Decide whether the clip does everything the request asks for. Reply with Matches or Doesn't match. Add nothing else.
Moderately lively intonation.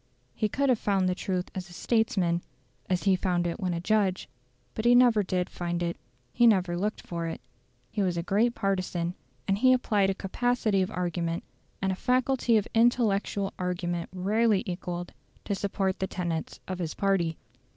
Matches